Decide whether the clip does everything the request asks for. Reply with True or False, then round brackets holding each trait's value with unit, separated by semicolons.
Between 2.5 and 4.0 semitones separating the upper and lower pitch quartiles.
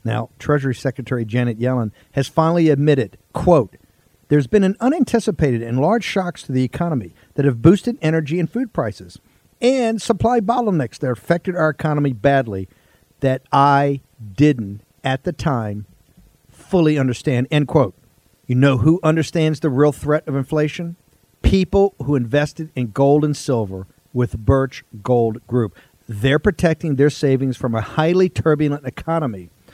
False (4.6 semitones)